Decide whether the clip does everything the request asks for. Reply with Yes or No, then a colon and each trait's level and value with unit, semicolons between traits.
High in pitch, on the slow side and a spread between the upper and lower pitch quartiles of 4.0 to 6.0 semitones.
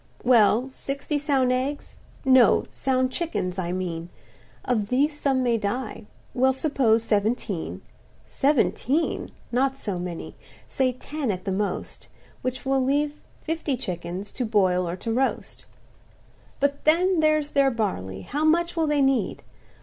Yes: very high, 255 Hz; slow, 125 wpm; wide, 5.4 semitones